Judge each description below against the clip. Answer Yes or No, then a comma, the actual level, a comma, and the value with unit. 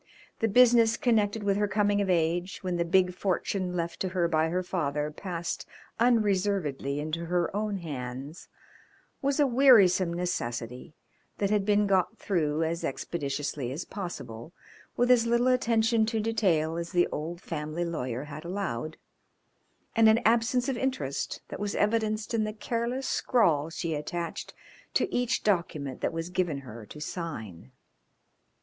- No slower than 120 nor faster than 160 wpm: Yes, average, 155 wpm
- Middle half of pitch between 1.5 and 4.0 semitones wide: No, wide, 5.6 semitones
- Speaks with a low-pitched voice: No, medium, 180 Hz